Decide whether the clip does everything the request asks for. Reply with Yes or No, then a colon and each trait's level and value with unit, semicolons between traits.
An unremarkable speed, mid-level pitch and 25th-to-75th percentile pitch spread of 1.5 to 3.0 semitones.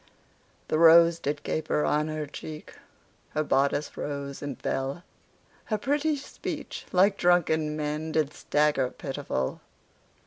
No: slow, 125 wpm; medium, 150 Hz; average, 2.7 semitones